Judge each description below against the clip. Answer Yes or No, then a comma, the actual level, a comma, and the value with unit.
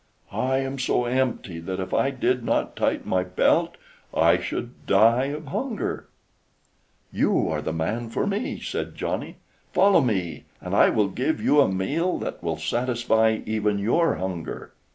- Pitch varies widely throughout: Yes, wide, 6.0 semitones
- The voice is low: Yes, low, 120 Hz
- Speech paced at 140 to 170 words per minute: Yes, average, 160 wpm